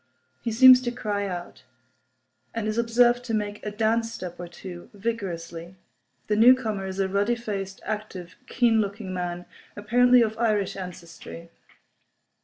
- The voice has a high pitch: Yes, high, 210 Hz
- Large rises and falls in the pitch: No, average, 3.7 semitones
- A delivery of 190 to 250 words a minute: No, average, 145 wpm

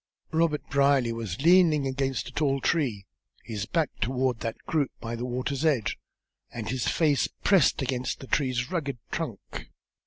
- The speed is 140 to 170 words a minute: Yes, average, 155 wpm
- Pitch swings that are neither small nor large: Yes, average, 3.7 semitones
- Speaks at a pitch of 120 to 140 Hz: Yes, low, 135 Hz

